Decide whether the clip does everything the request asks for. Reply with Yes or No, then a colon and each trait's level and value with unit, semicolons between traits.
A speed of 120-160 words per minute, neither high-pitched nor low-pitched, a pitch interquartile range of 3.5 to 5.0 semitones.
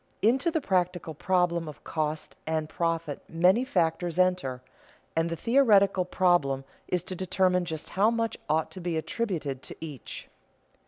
No: average, 155 wpm; medium, 175 Hz; average, 2.9 semitones